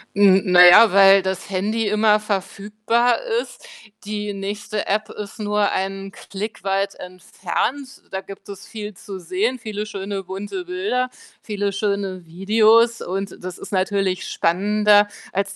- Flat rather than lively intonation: Yes, narrow, 1.7 semitones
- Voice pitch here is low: No, high, 200 Hz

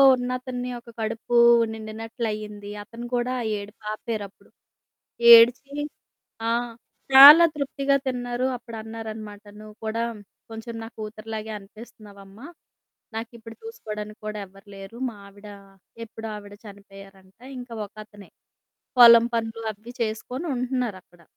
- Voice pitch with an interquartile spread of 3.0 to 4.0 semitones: No, narrow, 2.4 semitones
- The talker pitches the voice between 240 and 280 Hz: No, high, 220 Hz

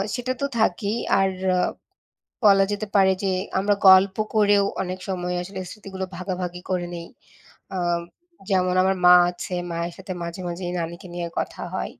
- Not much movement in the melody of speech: Yes, narrow, 1.9 semitones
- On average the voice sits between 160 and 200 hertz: Yes, high, 190 Hz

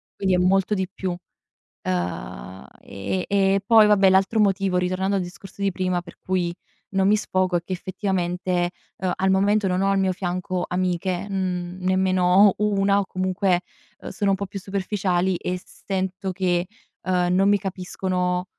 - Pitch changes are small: Yes, narrow, 1.4 semitones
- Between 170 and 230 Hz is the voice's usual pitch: Yes, medium, 185 Hz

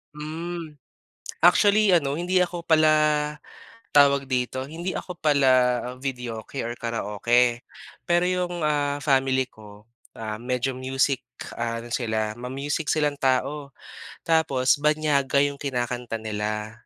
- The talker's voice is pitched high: No, medium, 140 Hz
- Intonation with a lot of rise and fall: No, average, 4.1 semitones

